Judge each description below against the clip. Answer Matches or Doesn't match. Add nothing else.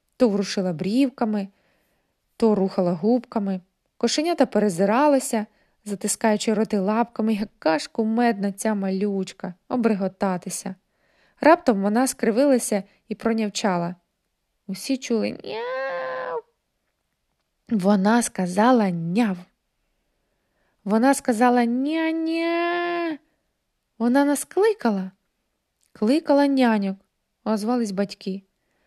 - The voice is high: Matches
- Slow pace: Matches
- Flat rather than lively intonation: Doesn't match